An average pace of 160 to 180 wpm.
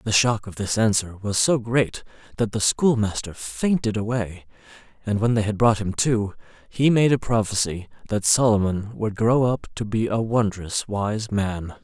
Yes: average, 175 wpm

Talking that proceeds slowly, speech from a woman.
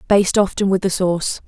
No: fast, 205 wpm; female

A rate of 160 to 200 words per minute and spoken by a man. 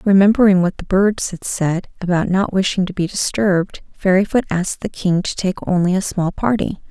No: average, 190 wpm; female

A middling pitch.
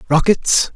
Yes: medium, 170 Hz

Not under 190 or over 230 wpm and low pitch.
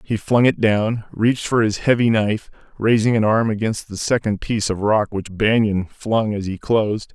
Yes: average, 200 wpm; low, 110 Hz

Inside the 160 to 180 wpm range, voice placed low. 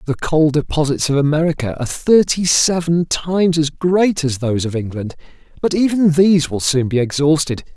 No: average, 170 wpm; medium, 155 Hz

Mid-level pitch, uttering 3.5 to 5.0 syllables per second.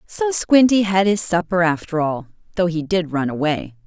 Yes: medium, 175 Hz; 4.8 syllables/s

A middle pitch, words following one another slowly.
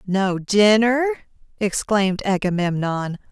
No: high, 200 Hz; slow, 70 wpm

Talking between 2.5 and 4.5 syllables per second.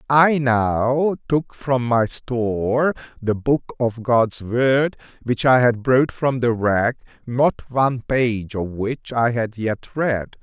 Yes: 3.2 syllables/s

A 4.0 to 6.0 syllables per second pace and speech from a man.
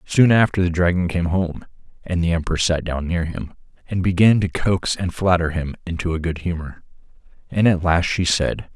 Yes: 5.0 syllables/s; male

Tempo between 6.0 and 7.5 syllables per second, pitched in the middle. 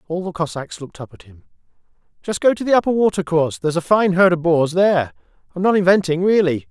Yes: 6.5 syllables/s; medium, 170 Hz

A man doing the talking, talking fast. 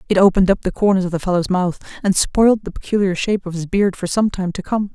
No: female; fast, 265 wpm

